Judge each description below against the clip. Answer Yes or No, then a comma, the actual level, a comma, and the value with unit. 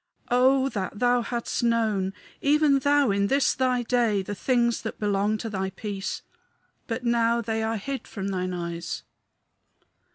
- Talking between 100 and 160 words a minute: Yes, average, 155 wpm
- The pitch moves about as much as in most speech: Yes, average, 3.8 semitones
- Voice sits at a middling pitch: No, high, 225 Hz